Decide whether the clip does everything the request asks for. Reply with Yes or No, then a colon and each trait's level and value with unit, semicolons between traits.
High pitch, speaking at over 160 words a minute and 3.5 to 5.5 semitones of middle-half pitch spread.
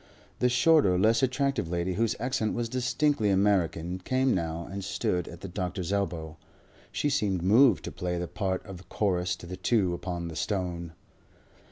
No: very low, 95 Hz; average, 170 wpm; average, 4.6 semitones